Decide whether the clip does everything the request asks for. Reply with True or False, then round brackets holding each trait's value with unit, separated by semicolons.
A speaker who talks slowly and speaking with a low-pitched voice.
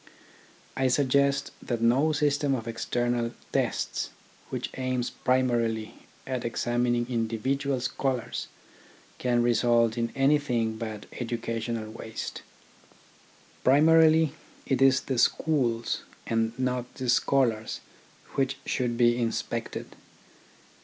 True (100 wpm; 120 Hz)